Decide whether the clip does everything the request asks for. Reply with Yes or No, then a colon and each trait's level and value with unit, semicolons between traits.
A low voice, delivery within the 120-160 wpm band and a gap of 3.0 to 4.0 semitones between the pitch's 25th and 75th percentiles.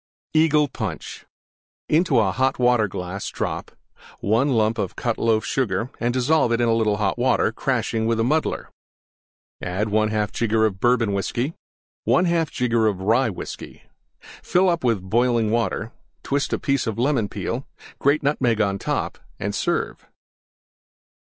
Yes: low, 115 Hz; slow, 135 wpm; average, 3.5 semitones